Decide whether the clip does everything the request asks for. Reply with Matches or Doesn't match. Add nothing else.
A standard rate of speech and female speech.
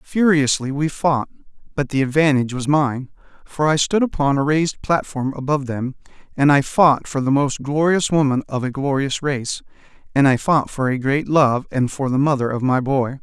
Doesn't match